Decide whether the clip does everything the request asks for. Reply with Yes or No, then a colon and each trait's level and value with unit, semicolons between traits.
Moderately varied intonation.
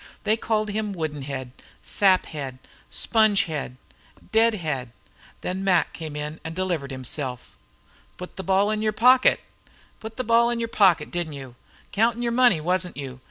No: wide, 6.6 semitones